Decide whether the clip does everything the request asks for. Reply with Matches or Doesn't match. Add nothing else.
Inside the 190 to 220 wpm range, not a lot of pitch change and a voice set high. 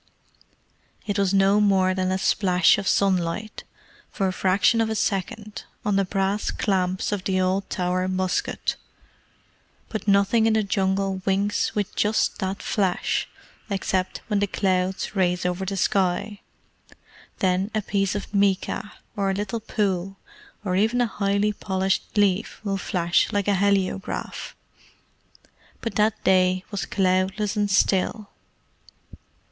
Doesn't match